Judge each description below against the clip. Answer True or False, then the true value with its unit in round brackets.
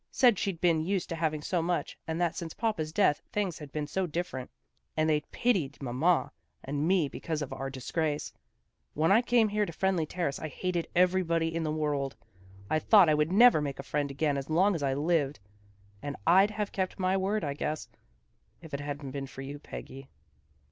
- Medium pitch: True (160 Hz)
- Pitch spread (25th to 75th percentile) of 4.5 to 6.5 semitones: False (4.1 semitones)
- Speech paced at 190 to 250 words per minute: True (205 wpm)